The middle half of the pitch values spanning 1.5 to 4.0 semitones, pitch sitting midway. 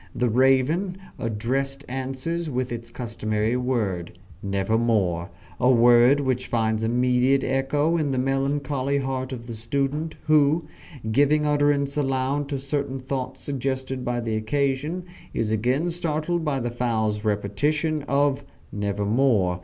No: average, 3.5 semitones; low, 130 Hz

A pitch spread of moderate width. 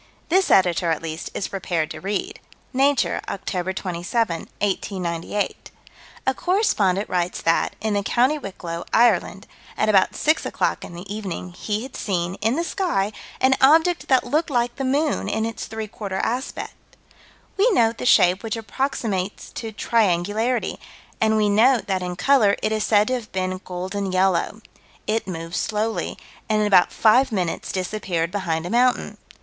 Yes: average, 4.6 semitones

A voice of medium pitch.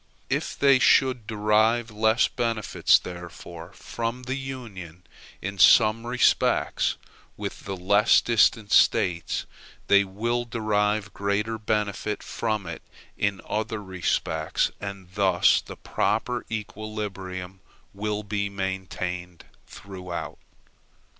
No: low, 105 Hz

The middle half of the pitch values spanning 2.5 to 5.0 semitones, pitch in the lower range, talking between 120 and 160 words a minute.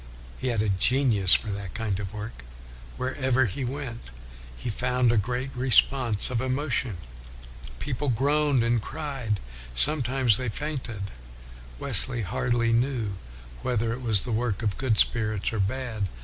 Yes: average, 3.5 semitones; low, 120 Hz; average, 145 wpm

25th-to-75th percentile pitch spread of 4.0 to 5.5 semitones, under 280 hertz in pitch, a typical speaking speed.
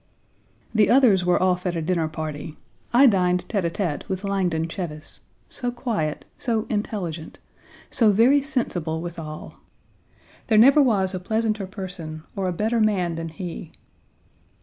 Yes: average, 4.7 semitones; medium, 185 Hz; average, 150 wpm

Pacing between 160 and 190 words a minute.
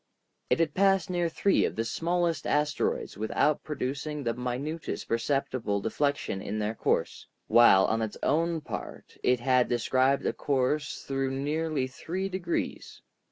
No: average, 145 wpm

